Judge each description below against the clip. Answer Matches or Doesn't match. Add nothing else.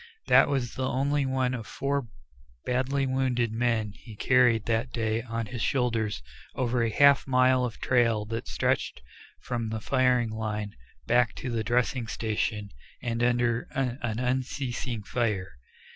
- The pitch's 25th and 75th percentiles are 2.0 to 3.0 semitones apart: Matches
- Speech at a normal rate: Matches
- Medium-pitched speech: Doesn't match